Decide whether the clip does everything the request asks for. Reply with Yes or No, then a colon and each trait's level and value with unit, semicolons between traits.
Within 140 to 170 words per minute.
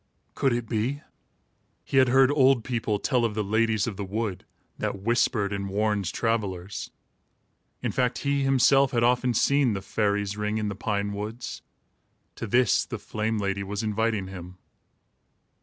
Yes: average, 160 wpm